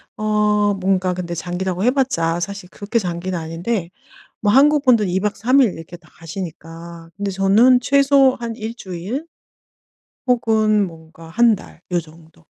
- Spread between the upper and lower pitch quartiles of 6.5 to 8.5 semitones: No, average, 5.2 semitones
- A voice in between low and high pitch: No, high, 195 Hz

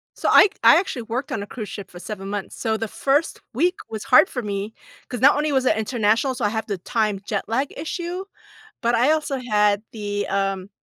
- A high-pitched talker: Yes, high, 225 Hz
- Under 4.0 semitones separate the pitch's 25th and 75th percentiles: No, average, 4.6 semitones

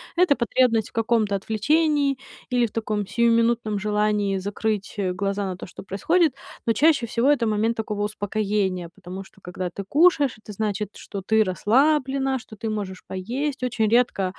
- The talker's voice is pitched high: Yes, high, 215 Hz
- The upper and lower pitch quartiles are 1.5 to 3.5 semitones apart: No, average, 3.9 semitones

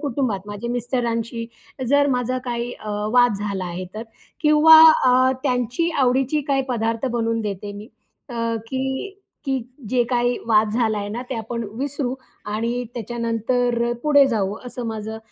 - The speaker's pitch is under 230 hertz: No, high, 240 Hz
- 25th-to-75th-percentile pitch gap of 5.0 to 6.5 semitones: No, average, 2.8 semitones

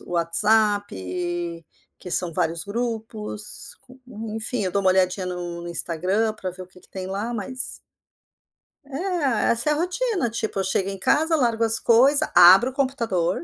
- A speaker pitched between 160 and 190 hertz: No, high, 215 Hz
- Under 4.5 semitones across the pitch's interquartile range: No, average, 4.8 semitones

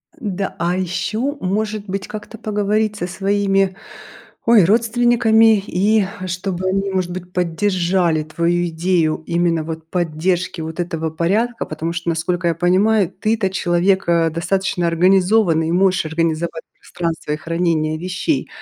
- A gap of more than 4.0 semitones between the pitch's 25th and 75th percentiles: No, average, 3.3 semitones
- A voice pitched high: No, medium, 180 Hz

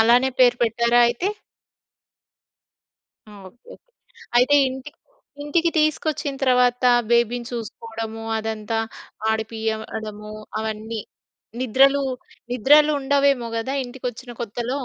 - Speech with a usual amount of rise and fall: Yes, average, 3.2 semitones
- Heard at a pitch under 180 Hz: No, high, 240 Hz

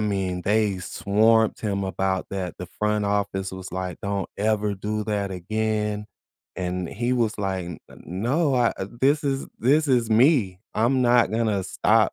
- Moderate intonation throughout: Yes, average, 3.2 semitones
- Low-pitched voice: Yes, low, 105 Hz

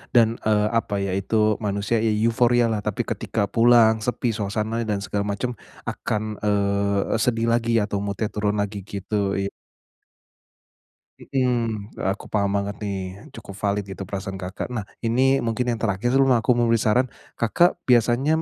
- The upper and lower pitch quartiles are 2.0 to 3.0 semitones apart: Yes, average, 2.7 semitones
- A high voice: No, low, 110 Hz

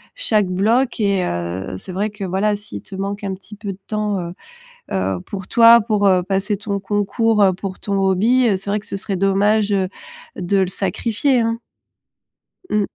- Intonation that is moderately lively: No, narrow, 1.9 semitones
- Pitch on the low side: No, high, 200 Hz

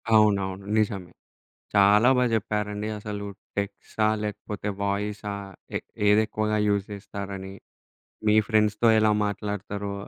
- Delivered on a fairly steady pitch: Yes, narrow, 1.1 semitones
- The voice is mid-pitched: No, low, 105 Hz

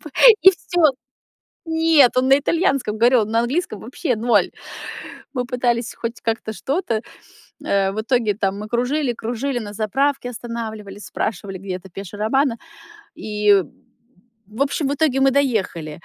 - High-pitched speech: Yes, high, 235 Hz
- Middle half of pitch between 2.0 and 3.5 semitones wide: No, average, 4.4 semitones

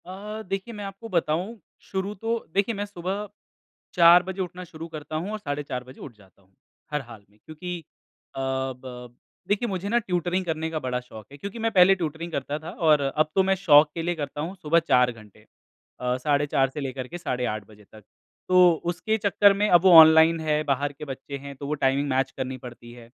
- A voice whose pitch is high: No, medium, 160 Hz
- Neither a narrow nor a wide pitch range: No, wide, 6.0 semitones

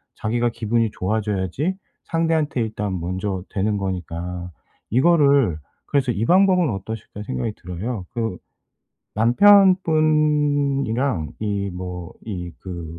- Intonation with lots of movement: Yes, wide, 7.6 semitones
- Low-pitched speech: Yes, low, 110 Hz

